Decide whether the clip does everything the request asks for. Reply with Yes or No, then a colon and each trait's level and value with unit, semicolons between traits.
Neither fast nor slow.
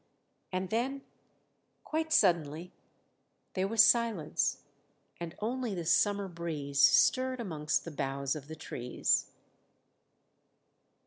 No: slow, 105 wpm